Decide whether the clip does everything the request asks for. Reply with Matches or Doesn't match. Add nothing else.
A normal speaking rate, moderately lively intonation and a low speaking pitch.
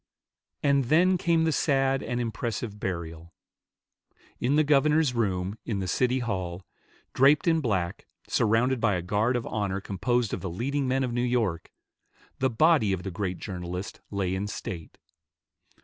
Doesn't match